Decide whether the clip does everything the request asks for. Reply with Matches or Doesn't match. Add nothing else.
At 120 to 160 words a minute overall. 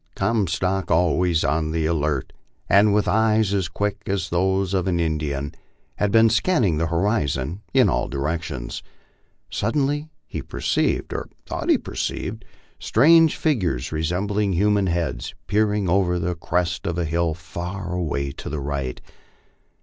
Matches